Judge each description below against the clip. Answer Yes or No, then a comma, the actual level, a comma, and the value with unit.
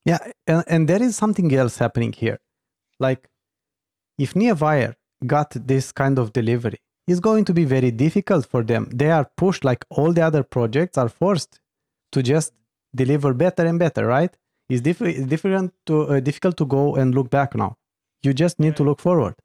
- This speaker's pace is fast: No, average, 185 wpm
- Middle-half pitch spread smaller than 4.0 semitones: No, average, 5.0 semitones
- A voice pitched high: No, medium, 145 Hz